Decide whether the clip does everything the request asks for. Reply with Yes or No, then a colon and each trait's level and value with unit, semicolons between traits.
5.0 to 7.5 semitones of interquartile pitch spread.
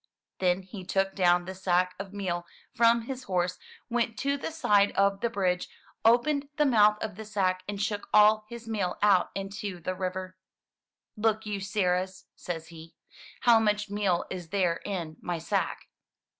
No: average, 3.0 semitones